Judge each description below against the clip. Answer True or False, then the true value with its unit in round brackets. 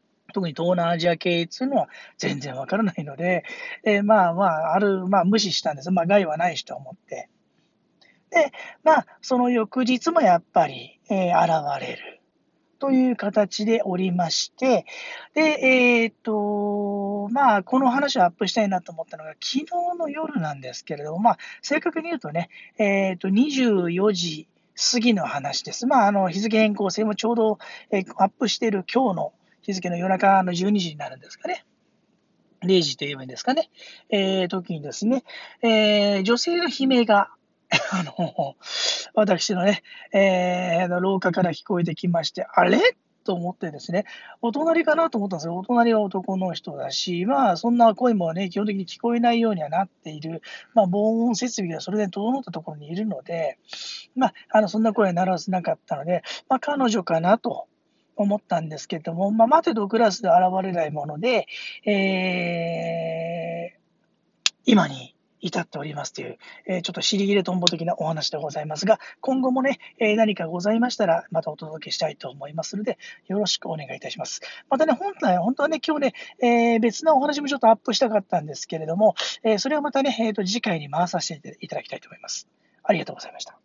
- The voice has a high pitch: True (205 Hz)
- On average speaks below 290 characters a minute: False (350 characters per minute)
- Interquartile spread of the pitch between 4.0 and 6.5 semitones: True (5.3 semitones)